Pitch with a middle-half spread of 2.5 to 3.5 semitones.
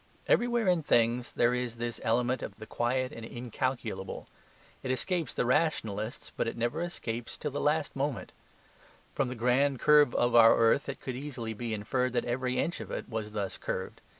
Yes: average, 3.1 semitones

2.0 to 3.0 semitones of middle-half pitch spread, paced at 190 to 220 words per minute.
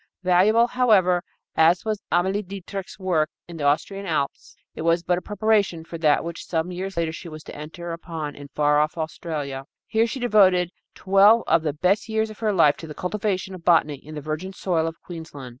No: average, 3.8 semitones; fast, 205 wpm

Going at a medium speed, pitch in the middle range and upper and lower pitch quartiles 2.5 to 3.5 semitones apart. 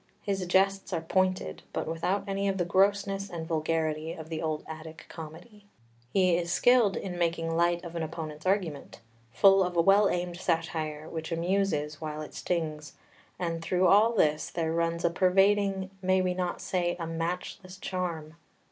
Yes: average, 170 wpm; medium, 175 Hz; average, 2.8 semitones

